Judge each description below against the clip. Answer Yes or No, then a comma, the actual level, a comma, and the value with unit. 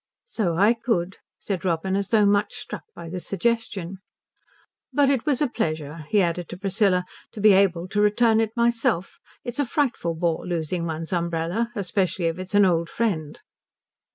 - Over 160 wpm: Yes, average, 175 wpm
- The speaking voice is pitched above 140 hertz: Yes, high, 190 Hz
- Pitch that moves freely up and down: No, average, 4.9 semitones